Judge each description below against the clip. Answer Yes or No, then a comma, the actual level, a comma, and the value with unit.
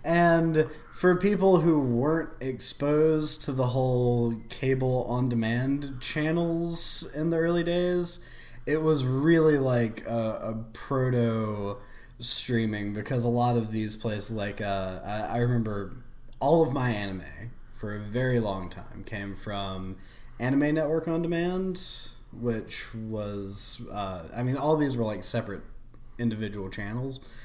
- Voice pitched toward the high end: No, low, 120 Hz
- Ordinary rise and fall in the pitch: No, wide, 5.9 semitones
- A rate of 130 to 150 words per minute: Yes, average, 140 wpm